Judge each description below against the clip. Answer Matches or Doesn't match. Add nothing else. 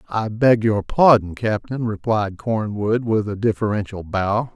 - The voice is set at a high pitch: Doesn't match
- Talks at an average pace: Matches